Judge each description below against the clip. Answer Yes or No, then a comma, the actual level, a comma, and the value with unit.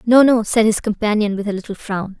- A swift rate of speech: Yes, fast, 245 wpm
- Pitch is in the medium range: No, high, 215 Hz